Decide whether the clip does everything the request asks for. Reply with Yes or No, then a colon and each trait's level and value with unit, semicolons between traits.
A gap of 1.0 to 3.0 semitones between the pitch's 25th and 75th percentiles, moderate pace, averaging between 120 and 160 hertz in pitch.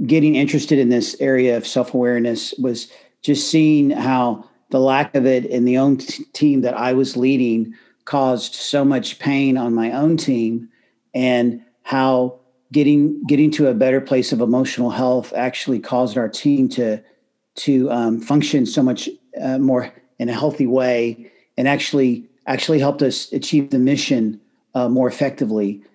Yes: narrow, 2.6 semitones; average, 165 wpm; low, 130 Hz